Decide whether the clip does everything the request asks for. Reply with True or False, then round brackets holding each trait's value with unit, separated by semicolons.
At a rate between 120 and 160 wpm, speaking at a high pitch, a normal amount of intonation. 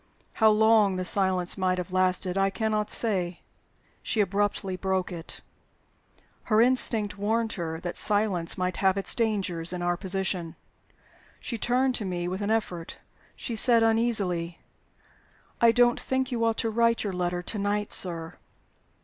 True (155 wpm; 200 Hz; 3.6 semitones)